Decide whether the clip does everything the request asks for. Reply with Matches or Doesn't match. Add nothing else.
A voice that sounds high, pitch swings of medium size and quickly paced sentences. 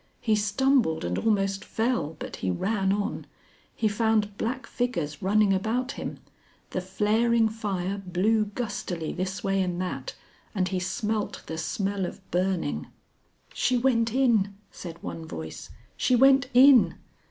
Doesn't match